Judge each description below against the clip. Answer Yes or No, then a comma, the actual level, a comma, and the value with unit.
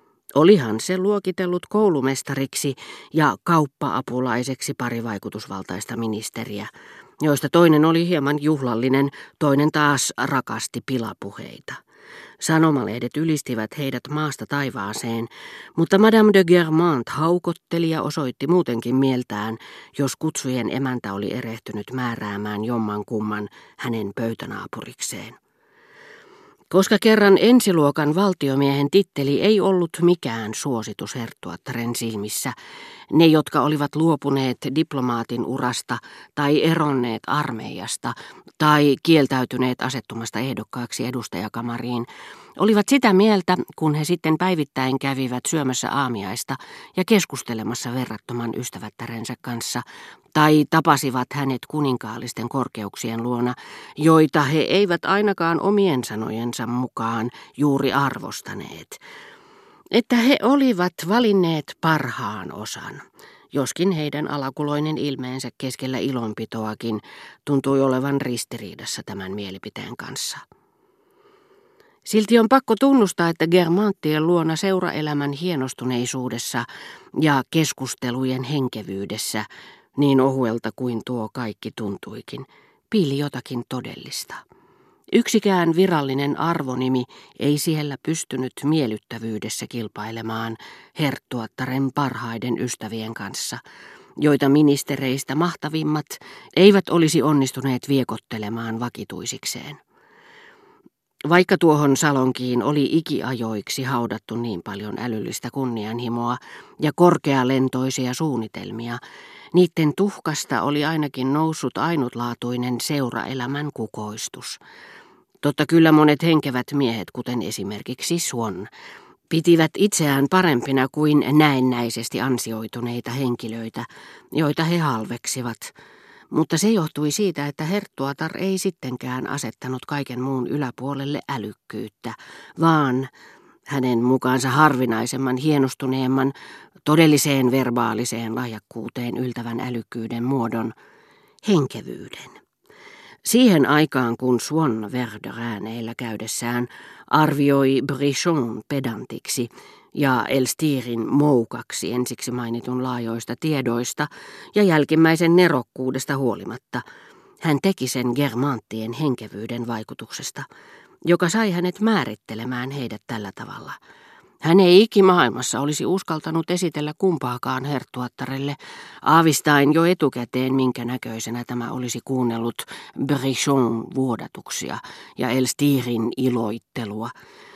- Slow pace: Yes, slow, 90 wpm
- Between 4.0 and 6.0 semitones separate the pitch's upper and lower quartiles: Yes, average, 4.8 semitones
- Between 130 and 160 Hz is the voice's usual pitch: Yes, low, 135 Hz